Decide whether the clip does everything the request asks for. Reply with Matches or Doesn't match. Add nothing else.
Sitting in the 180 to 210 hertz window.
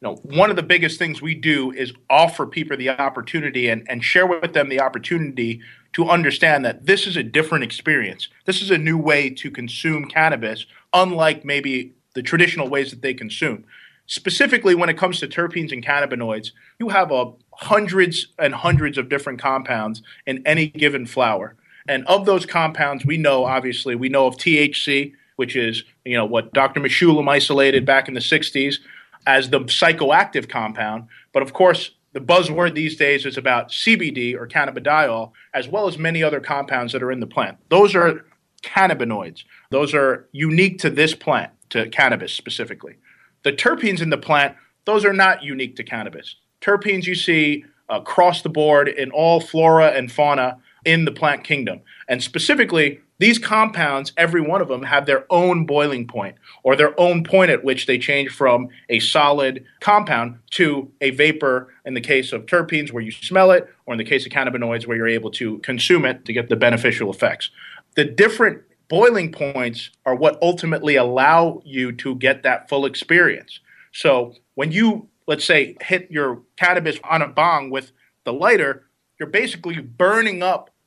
Doesn't match